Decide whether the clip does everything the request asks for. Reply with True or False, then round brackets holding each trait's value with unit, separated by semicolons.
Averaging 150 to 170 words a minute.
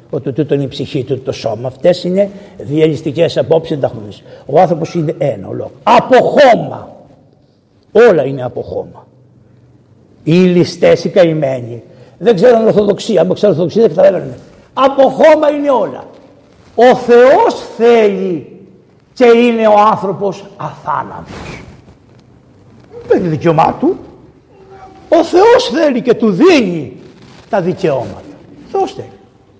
False (130 wpm)